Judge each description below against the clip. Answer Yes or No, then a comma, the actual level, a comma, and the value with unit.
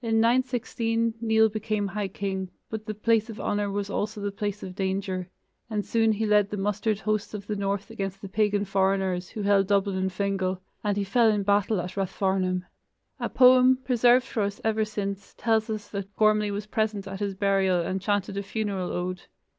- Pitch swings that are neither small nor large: No, narrow, 2.0 semitones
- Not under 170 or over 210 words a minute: Yes, average, 195 wpm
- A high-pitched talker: Yes, high, 205 Hz